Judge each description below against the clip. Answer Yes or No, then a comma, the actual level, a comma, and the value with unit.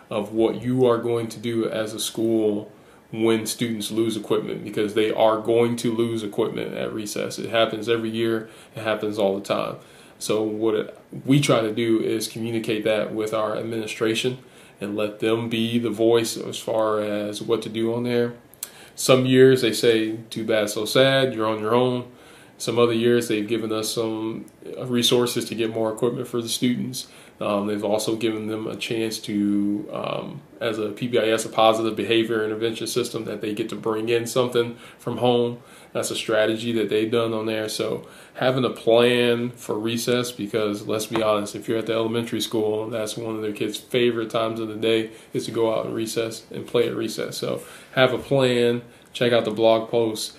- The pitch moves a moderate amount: No, narrow, 1.5 semitones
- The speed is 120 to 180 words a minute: No, average, 195 wpm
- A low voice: Yes, low, 115 Hz